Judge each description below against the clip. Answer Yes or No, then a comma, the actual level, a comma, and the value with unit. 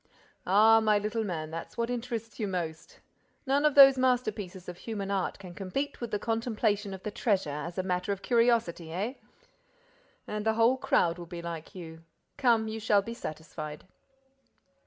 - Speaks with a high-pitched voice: Yes, high, 210 Hz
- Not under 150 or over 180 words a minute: Yes, average, 165 wpm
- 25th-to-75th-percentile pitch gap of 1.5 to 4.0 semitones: No, average, 4.7 semitones